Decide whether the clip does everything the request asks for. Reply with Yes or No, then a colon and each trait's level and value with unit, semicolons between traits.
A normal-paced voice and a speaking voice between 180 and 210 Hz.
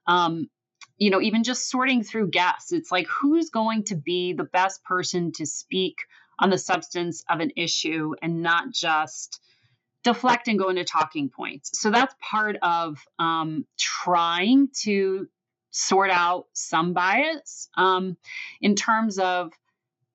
Yes: average, 145 wpm; medium, 185 Hz